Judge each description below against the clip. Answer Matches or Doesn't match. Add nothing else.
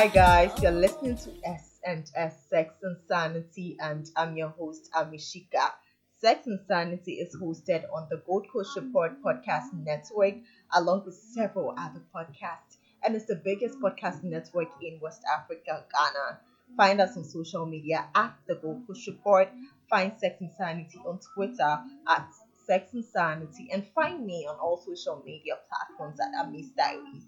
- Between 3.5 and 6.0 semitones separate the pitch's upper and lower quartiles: Matches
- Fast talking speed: Doesn't match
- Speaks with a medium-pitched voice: Matches